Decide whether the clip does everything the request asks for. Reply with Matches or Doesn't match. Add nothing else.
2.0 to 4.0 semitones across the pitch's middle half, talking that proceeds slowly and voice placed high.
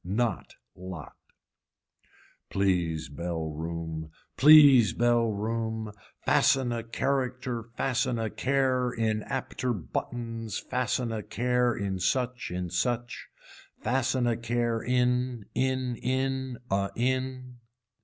Doesn't match